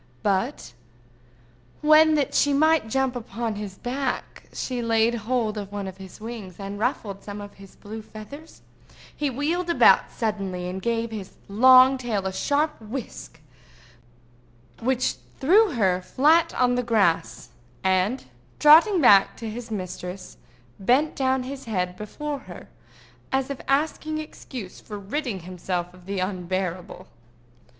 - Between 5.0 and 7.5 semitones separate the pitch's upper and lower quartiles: Yes, wide, 5.6 semitones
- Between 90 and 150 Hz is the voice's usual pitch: No, high, 225 Hz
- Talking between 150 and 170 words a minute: No, average, 140 wpm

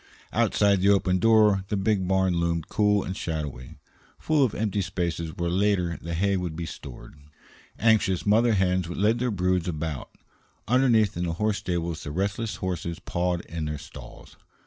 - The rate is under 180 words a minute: Yes, average, 170 wpm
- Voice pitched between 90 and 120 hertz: Yes, very low, 95 Hz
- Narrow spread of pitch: No, average, 3.4 semitones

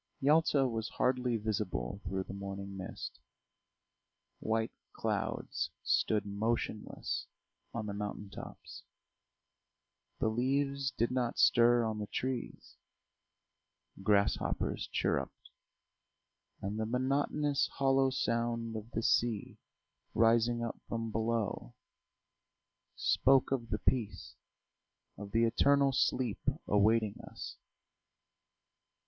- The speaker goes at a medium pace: No, slow, 100 wpm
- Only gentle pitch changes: No, average, 3.4 semitones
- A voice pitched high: No, low, 115 Hz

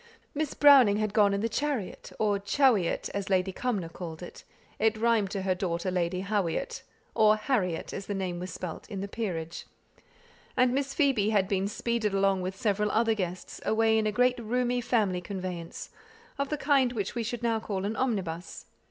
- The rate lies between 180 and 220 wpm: Yes, average, 185 wpm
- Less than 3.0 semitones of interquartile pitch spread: No, average, 4.0 semitones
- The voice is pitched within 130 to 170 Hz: No, high, 205 Hz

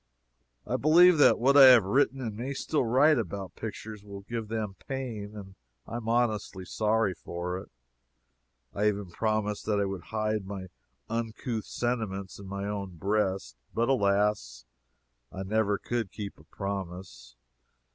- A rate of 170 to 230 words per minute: No, average, 155 wpm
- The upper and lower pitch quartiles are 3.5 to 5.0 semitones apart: No, average, 3.1 semitones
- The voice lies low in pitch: Yes, low, 105 Hz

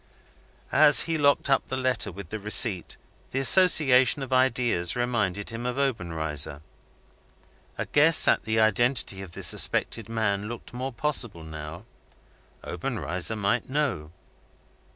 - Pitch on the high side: No, low, 115 Hz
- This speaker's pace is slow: Yes, slow, 130 wpm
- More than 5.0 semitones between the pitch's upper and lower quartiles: Yes, wide, 5.6 semitones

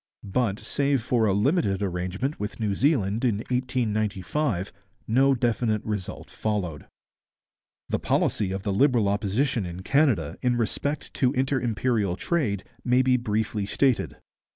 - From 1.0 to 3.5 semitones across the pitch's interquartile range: No, average, 4.4 semitones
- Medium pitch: No, low, 110 Hz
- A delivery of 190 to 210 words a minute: No, slow, 135 wpm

